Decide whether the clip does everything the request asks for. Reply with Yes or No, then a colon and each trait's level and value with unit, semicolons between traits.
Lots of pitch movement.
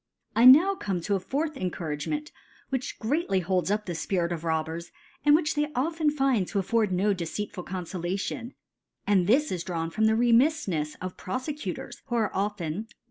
Yes: wide, 6.8 semitones